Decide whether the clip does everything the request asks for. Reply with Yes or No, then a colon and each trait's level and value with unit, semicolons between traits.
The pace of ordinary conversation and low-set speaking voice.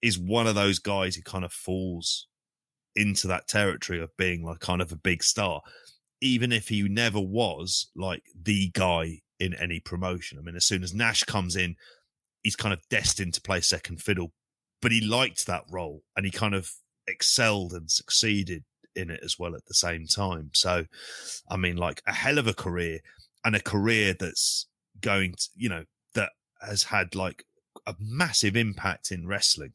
Yes: average, 190 wpm; very low, 95 Hz